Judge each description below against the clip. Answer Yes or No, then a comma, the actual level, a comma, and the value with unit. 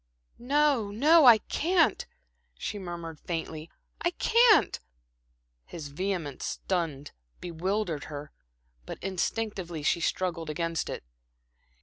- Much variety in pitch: Yes, wide, 5.7 semitones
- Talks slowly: Yes, slow, 100 wpm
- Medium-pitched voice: Yes, medium, 180 Hz